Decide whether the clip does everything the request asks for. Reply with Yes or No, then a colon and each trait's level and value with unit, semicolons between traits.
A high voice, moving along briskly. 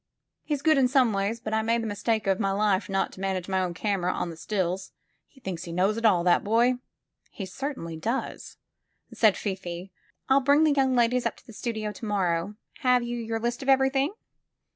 Yes: high, 215 Hz; fast, 210 wpm